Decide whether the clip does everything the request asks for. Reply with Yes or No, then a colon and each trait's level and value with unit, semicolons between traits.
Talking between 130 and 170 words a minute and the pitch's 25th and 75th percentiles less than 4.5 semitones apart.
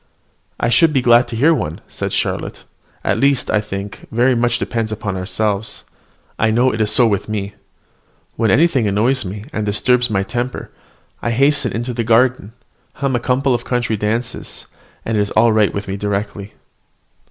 No: average, 180 wpm; average, 3.1 semitones